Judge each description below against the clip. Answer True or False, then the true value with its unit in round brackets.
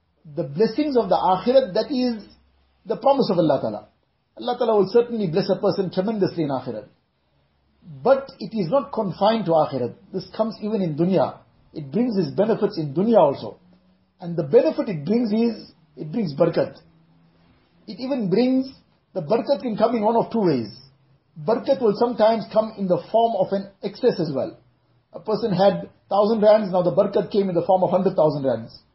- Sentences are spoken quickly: False (185 wpm)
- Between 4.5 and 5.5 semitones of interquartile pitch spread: True (4.9 semitones)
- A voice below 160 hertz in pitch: False (200 Hz)